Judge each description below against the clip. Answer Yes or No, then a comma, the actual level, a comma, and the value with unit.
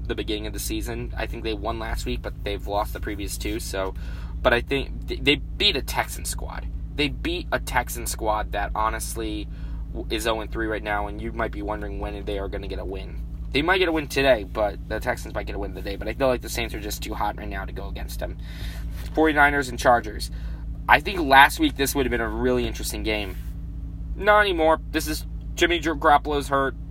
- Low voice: Yes, low, 105 Hz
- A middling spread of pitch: No, wide, 6.3 semitones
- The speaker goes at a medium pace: No, fast, 225 wpm